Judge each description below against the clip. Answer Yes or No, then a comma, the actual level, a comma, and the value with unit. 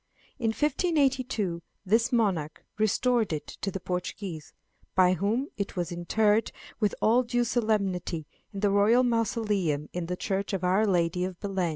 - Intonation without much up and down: No, average, 4.1 semitones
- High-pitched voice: Yes, high, 200 Hz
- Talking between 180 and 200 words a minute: No, average, 155 wpm